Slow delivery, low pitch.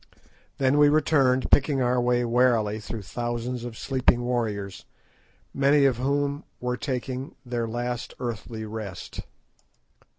Yes: slow, 125 wpm; low, 125 Hz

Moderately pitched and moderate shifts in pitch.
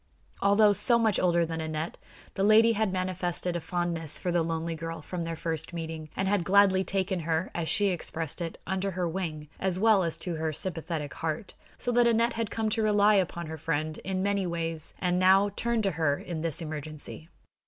Yes: medium, 175 Hz; average, 3.4 semitones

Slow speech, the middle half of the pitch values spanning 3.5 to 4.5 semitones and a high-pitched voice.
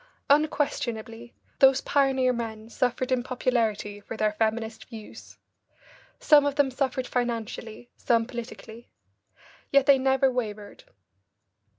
No: slow, 110 wpm; average, 3.0 semitones; high, 245 Hz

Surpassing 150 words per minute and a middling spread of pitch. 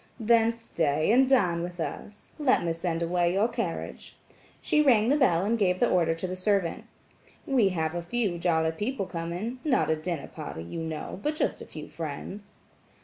No: average, 185 wpm; wide, 5.7 semitones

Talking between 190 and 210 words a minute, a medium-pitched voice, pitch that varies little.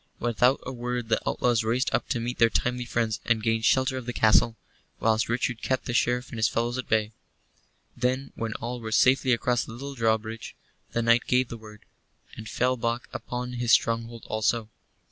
No: average, 200 wpm; low, 120 Hz; narrow, 1.7 semitones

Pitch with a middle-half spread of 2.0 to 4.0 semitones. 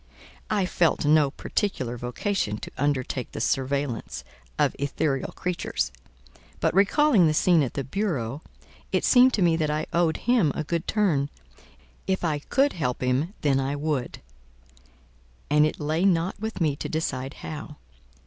No: average, 4.8 semitones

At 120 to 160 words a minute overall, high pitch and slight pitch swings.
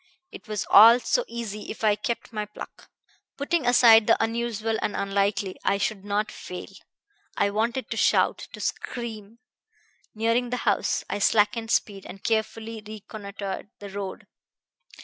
Yes: average, 150 wpm; high, 215 Hz; narrow, 2.2 semitones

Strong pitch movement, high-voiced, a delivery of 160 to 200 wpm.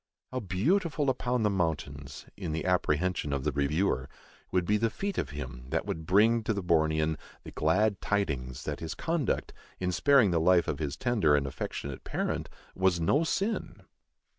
No: wide, 6.8 semitones; very low, 90 Hz; average, 175 wpm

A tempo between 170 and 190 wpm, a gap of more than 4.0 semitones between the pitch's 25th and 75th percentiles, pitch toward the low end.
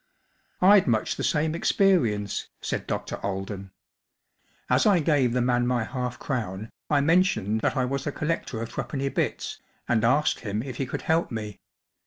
Yes: average, 175 wpm; average, 5.3 semitones; low, 125 Hz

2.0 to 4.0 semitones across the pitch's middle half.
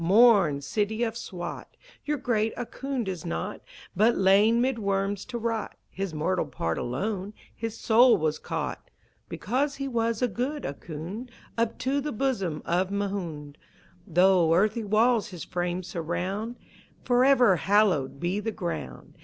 No: average, 5.0 semitones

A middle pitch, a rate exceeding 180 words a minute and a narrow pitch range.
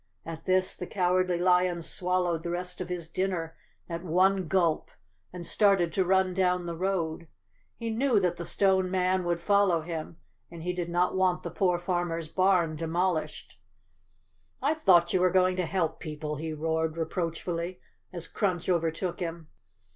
No: medium, 180 Hz; average, 170 wpm; narrow, 1.8 semitones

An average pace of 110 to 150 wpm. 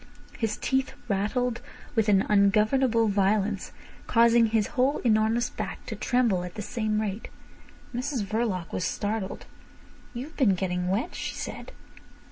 Yes: slow, 135 wpm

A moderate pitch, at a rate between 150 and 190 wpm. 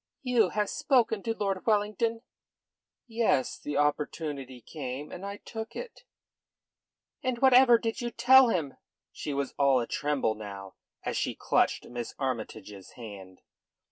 No: medium, 165 Hz; average, 140 wpm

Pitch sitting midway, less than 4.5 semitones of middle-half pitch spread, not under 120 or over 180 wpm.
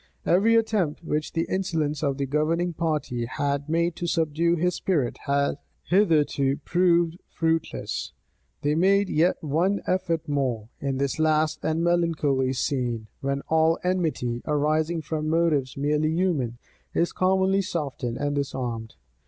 Yes: medium, 155 Hz; average, 3.5 semitones; slow, 135 wpm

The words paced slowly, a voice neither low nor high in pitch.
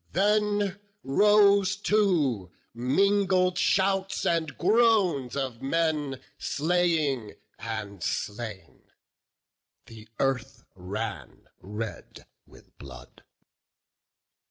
Yes: slow, 75 wpm; medium, 155 Hz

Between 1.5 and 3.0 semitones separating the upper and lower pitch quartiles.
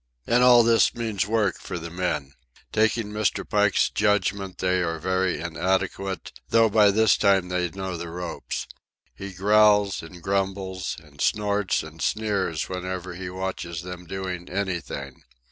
Yes: narrow, 2.6 semitones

